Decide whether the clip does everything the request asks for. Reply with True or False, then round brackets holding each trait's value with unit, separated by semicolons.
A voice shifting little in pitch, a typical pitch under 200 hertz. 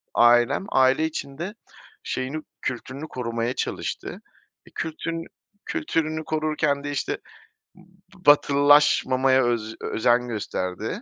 False (4.4 semitones; 140 Hz)